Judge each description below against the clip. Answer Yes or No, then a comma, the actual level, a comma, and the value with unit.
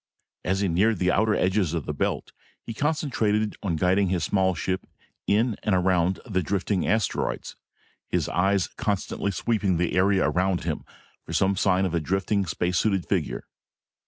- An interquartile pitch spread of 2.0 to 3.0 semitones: Yes, narrow, 2.4 semitones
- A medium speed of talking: Yes, average, 165 wpm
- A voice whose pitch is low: Yes, very low, 95 Hz